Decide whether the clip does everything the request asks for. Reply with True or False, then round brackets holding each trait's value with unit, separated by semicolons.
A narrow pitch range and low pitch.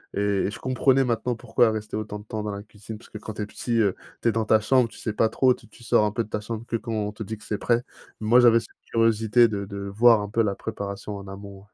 True (1.9 semitones; 110 Hz)